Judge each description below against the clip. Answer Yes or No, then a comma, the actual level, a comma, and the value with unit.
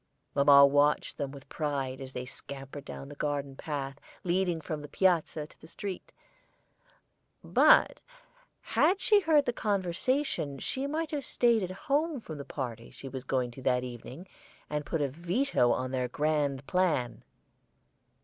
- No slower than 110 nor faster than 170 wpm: Yes, average, 160 wpm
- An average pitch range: No, wide, 5.9 semitones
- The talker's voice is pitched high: No, medium, 150 Hz